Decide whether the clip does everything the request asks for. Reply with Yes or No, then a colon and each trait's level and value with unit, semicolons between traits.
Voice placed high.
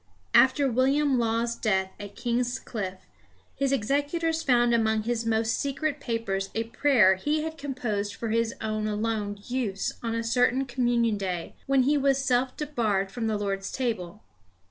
Yes: high, 235 Hz